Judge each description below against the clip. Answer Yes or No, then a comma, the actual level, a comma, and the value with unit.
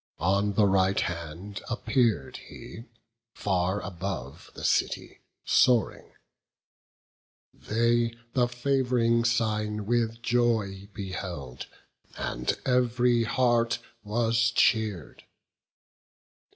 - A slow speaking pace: Yes, slow, 85 wpm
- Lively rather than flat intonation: No, average, 3.5 semitones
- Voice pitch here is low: Yes, low, 110 Hz